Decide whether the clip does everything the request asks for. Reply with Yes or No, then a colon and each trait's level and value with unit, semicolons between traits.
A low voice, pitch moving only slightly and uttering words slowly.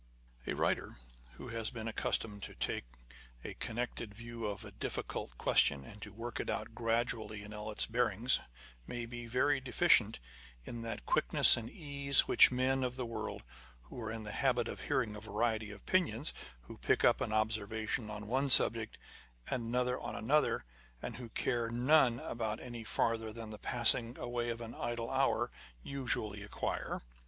No: low, 115 Hz; narrow, 2.3 semitones; average, 175 wpm